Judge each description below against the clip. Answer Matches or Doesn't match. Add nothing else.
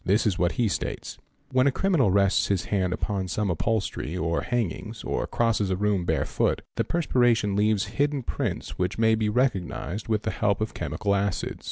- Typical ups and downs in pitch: Matches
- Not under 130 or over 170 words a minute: Doesn't match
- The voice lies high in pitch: Doesn't match